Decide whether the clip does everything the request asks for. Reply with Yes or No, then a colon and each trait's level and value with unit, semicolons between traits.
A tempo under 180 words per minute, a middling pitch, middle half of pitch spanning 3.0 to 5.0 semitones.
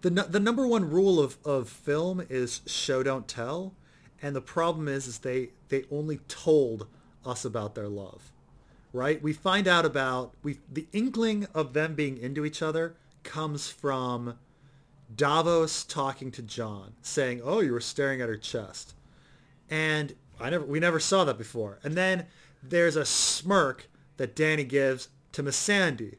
Yes: average, 165 wpm; medium, 145 Hz; average, 4.0 semitones